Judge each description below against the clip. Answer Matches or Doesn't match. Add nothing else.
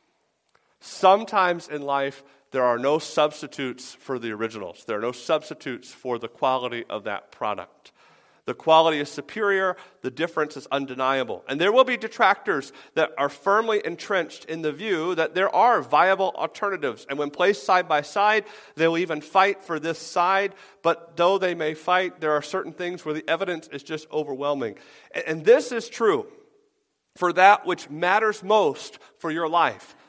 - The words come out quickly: Doesn't match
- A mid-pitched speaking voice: Matches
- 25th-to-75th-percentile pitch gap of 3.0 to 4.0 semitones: Doesn't match